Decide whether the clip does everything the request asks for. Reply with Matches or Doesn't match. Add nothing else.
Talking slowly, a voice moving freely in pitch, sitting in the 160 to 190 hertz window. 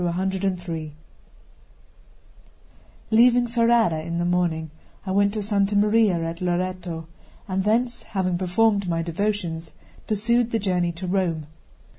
Doesn't match